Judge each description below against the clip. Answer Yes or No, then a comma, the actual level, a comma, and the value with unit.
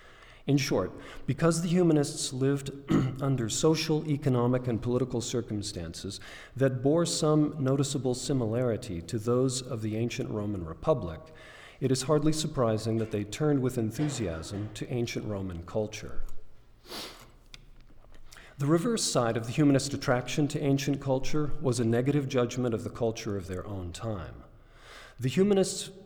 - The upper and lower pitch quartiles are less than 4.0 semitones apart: No, average, 4.8 semitones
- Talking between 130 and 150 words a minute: Yes, average, 140 wpm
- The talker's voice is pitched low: Yes, low, 125 Hz